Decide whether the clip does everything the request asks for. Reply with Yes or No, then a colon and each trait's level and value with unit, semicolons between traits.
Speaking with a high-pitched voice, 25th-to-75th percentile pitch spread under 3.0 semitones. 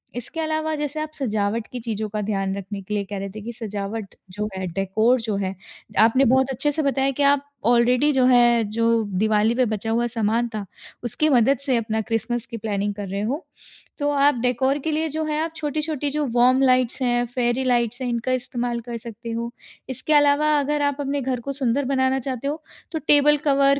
No: high, 245 Hz; average, 4.0 semitones